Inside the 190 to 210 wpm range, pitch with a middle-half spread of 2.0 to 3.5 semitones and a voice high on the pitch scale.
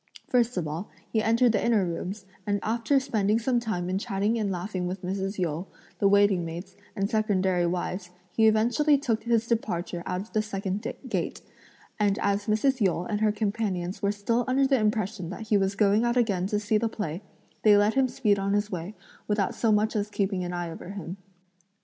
Yes: fast, 205 wpm; average, 2.9 semitones; high, 205 Hz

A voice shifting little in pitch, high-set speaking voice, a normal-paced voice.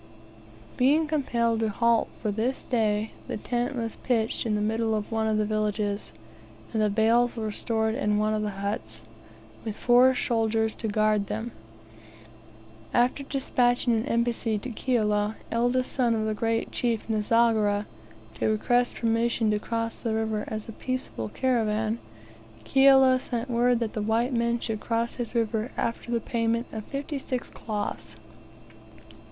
Yes: narrow, 2.0 semitones; high, 225 Hz; average, 160 wpm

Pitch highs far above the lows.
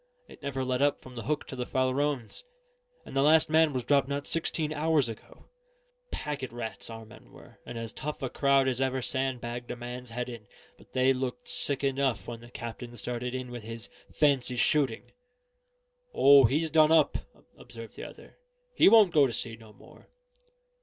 No: average, 3.2 semitones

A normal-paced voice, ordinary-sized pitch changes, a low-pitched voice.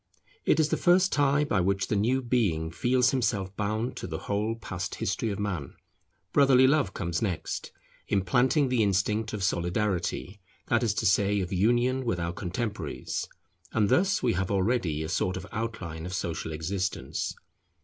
Yes: average, 170 wpm; average, 5.0 semitones; low, 105 Hz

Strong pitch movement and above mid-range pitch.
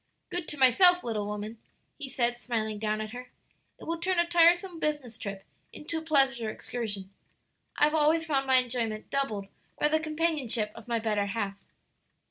Yes: wide, 6.3 semitones; very high, 250 Hz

